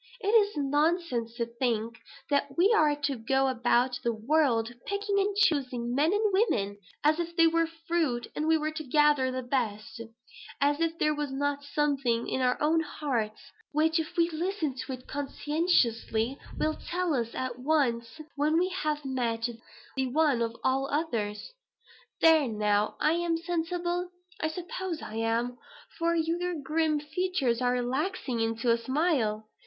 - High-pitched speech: Yes, very high, 290 Hz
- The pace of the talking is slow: No, average, 160 wpm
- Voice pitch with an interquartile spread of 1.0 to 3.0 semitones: No, average, 5.3 semitones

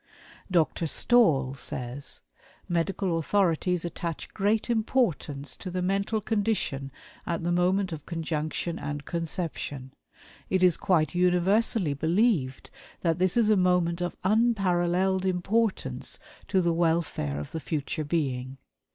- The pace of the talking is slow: Yes, slow, 125 wpm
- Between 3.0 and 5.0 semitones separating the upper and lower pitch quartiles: Yes, average, 3.6 semitones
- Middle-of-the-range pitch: Yes, medium, 175 Hz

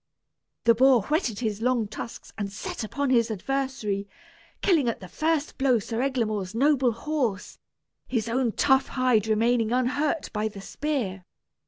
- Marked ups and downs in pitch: No, average, 3.8 semitones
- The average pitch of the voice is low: No, high, 240 Hz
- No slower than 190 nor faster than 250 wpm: No, average, 150 wpm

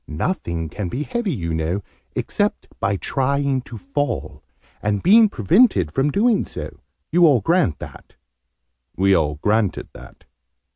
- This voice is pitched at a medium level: No, low, 120 Hz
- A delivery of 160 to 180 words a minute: No, average, 140 wpm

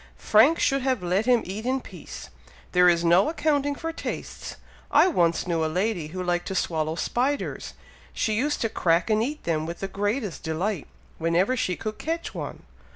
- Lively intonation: Yes, wide, 6.9 semitones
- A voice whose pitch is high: Yes, high, 205 Hz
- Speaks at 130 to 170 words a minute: No, average, 185 wpm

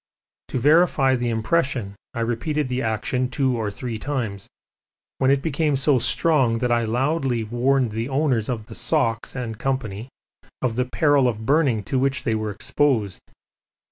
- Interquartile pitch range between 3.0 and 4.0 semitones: Yes, average, 3.4 semitones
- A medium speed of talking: Yes, average, 160 wpm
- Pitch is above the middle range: No, low, 125 Hz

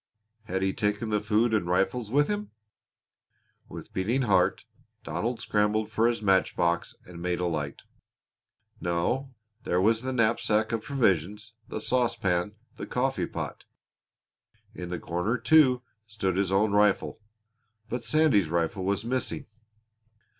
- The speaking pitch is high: No, low, 105 Hz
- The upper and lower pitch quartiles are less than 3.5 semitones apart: No, average, 4.3 semitones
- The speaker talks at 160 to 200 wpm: No, average, 140 wpm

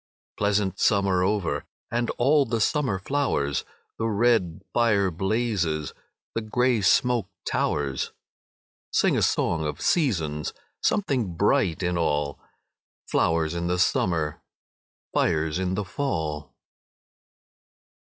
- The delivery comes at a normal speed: No, slow, 110 wpm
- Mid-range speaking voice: No, very low, 95 Hz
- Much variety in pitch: Yes, wide, 6.0 semitones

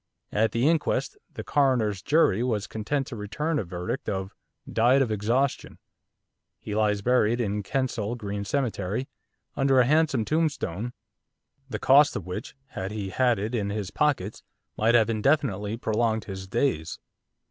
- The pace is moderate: Yes, average, 150 wpm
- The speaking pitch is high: No, low, 110 Hz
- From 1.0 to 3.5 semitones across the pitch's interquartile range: No, average, 4.4 semitones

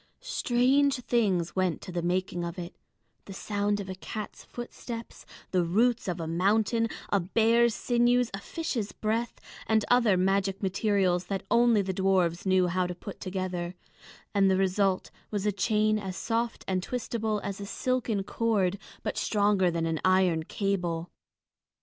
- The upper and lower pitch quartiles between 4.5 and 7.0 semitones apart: No, average, 3.5 semitones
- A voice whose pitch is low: No, high, 195 Hz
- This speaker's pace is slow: No, average, 160 wpm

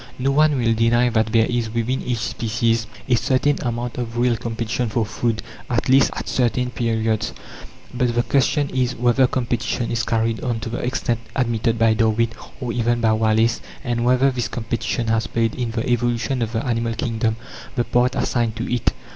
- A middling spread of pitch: No, narrow, 1.5 semitones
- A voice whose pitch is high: No, low, 120 Hz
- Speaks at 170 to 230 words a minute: Yes, average, 190 wpm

